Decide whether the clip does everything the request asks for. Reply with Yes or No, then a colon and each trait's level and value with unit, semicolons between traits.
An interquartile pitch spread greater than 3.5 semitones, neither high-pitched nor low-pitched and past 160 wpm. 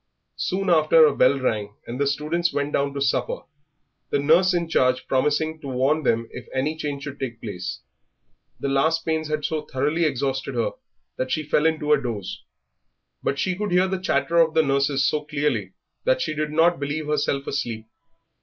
No: average, 3.0 semitones; medium, 145 Hz; average, 190 wpm